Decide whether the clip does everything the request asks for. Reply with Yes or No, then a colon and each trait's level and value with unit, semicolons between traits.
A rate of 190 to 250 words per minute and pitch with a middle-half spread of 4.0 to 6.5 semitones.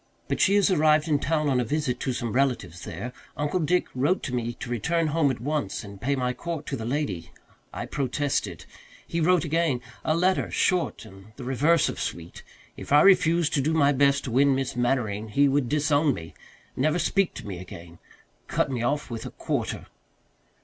Yes: average, 200 wpm; average, 4.5 semitones